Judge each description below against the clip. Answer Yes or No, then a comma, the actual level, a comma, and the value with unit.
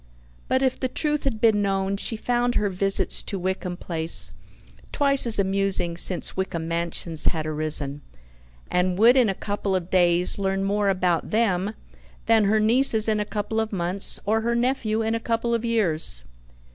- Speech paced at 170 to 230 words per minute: Yes, average, 175 wpm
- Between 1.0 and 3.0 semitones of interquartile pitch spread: No, average, 3.9 semitones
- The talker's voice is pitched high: Yes, high, 200 Hz